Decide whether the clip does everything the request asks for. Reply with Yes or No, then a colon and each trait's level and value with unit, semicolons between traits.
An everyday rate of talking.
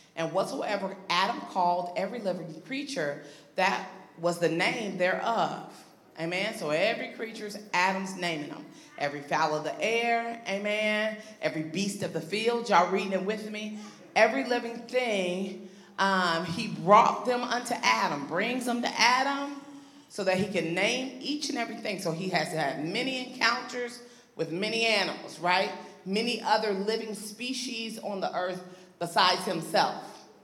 Yes: average, 150 wpm